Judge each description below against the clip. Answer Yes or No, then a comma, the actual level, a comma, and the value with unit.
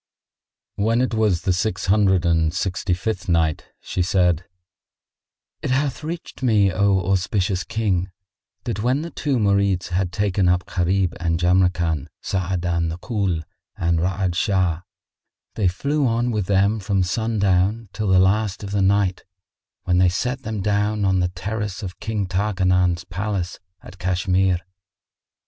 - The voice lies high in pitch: No, very low, 95 Hz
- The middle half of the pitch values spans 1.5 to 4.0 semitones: Yes, average, 2.8 semitones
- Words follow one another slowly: No, average, 150 wpm